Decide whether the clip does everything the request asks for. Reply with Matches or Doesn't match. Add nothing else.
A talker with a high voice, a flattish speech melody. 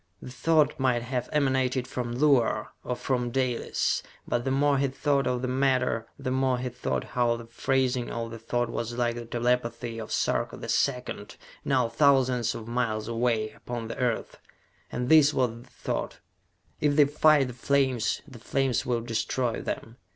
Doesn't match